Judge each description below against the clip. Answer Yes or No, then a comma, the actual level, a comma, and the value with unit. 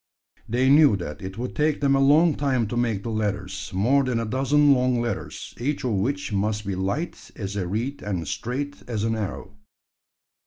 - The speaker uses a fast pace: No, average, 195 wpm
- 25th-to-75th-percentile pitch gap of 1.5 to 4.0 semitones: No, average, 5.3 semitones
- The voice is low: Yes, low, 115 Hz